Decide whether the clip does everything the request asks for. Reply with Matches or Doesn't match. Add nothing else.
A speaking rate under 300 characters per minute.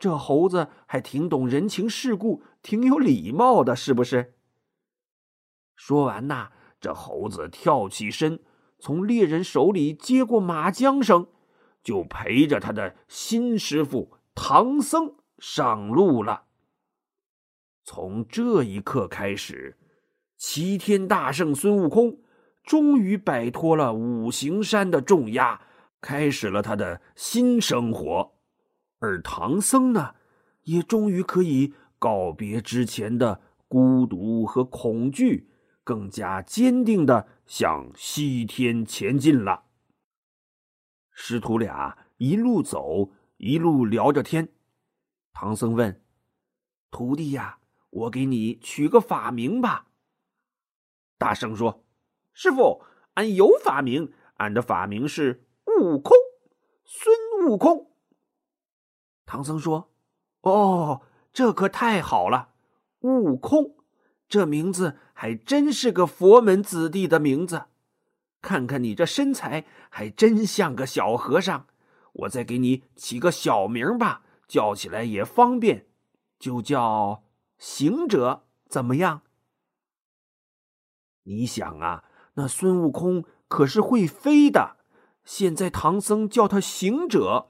Matches